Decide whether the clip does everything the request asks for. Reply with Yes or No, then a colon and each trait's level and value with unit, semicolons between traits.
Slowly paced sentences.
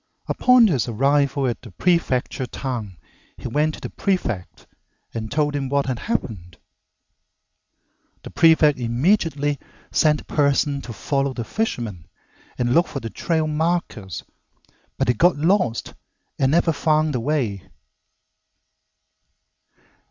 Yes: slow, 130 wpm